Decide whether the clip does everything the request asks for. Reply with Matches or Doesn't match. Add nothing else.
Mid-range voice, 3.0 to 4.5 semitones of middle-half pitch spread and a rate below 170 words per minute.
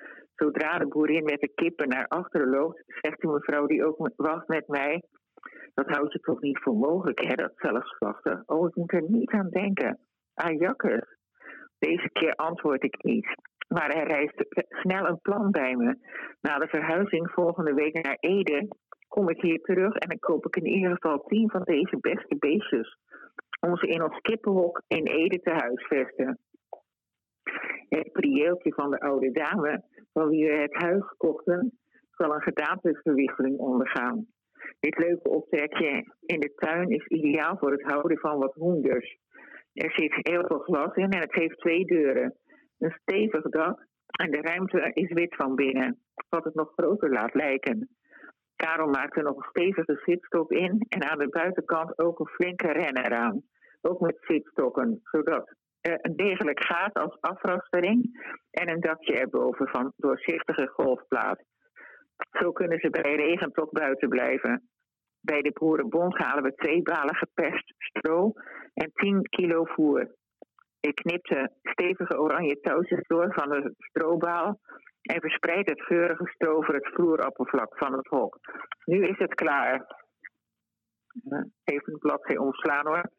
Matches